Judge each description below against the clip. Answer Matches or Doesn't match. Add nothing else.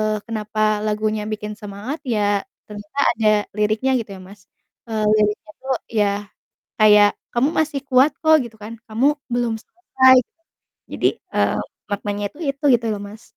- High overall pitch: Matches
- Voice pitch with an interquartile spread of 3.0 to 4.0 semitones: Matches